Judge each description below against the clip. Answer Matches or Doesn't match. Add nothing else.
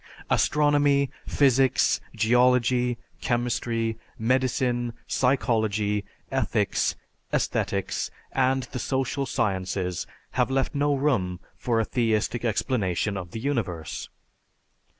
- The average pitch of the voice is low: Matches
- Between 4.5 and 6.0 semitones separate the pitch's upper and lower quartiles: Doesn't match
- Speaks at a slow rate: Matches